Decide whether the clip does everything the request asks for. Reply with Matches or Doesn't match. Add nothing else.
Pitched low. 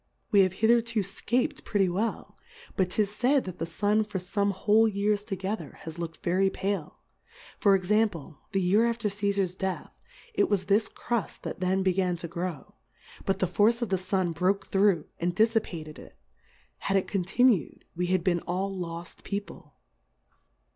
Doesn't match